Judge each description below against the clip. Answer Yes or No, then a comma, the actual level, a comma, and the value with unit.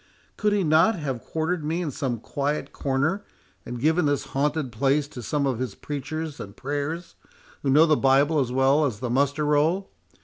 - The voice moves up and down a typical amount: Yes, average, 3.0 semitones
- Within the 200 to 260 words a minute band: No, average, 190 wpm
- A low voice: No, medium, 145 Hz